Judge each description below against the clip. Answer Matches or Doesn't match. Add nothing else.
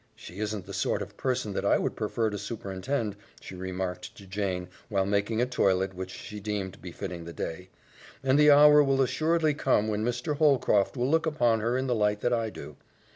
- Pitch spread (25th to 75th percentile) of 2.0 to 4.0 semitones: Doesn't match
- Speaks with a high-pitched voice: Doesn't match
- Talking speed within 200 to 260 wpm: Matches